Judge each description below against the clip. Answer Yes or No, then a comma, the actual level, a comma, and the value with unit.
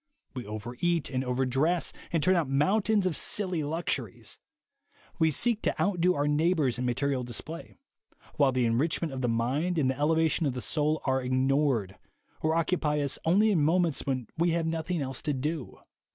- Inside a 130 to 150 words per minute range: No, average, 180 wpm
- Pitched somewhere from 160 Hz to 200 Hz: No, medium, 150 Hz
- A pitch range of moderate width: Yes, average, 4.4 semitones